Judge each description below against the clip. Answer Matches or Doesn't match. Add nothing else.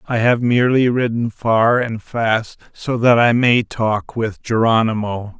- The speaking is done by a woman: Doesn't match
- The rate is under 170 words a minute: Matches